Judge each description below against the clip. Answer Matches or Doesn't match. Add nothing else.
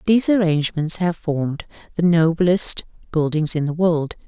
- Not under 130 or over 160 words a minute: Matches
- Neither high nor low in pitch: Matches